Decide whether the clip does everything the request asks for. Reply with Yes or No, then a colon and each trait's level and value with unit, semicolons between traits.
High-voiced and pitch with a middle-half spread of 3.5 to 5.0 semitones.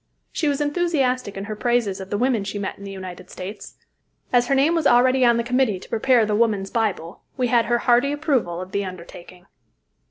Yes: high, 235 Hz; average, 4.7 semitones